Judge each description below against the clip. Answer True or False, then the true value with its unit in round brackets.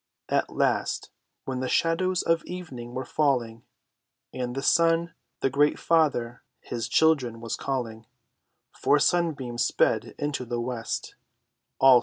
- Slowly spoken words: True (125 wpm)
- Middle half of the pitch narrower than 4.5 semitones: False (5.2 semitones)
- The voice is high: False (135 Hz)